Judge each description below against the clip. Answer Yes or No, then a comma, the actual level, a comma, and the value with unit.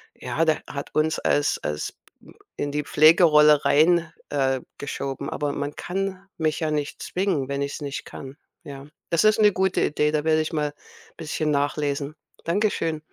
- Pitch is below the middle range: No, medium, 150 Hz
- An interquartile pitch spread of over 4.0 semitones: No, narrow, 2.5 semitones